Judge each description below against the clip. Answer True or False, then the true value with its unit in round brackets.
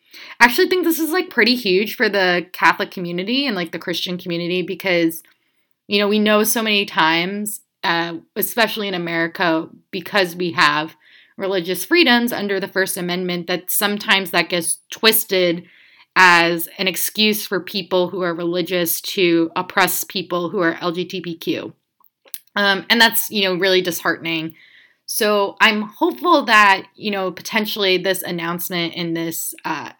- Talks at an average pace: True (150 wpm)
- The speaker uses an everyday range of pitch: True (3.3 semitones)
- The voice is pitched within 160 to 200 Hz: True (185 Hz)